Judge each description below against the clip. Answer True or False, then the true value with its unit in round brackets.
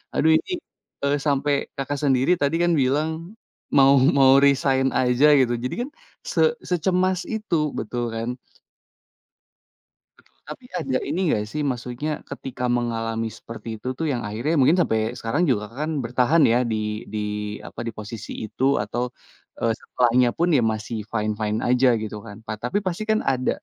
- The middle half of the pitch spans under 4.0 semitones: False (4.6 semitones)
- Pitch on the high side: False (130 Hz)